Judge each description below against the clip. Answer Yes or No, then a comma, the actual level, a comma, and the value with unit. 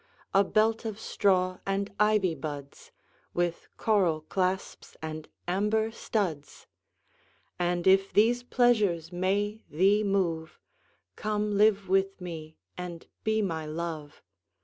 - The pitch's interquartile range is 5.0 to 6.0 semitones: No, average, 3.8 semitones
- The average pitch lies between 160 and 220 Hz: Yes, high, 190 Hz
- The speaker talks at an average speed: No, slow, 115 wpm